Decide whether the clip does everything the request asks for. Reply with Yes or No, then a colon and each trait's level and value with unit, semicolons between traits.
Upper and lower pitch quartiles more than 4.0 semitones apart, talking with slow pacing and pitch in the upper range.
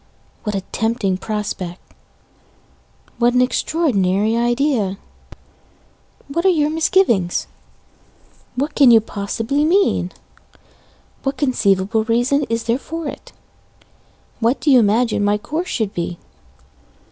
Yes: wide, 5.5 semitones; slow, 110 wpm; high, 235 Hz